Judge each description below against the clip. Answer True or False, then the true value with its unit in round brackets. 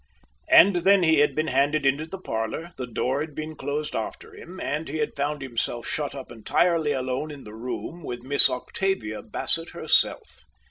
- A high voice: False (145 Hz)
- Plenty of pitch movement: False (3.6 semitones)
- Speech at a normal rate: True (185 wpm)